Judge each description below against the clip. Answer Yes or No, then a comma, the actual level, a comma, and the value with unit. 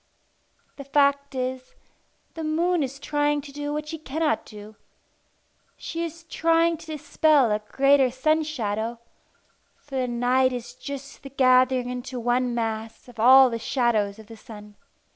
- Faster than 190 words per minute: No, average, 155 wpm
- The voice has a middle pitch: No, very high, 260 Hz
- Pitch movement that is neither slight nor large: Yes, average, 3.5 semitones